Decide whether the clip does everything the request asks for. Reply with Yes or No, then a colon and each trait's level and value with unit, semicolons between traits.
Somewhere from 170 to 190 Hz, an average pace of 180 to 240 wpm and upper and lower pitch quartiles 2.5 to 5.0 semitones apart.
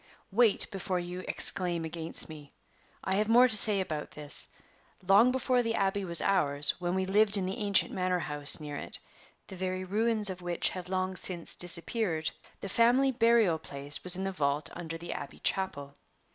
Yes: medium, 185 Hz; average, 185 wpm; average, 3.7 semitones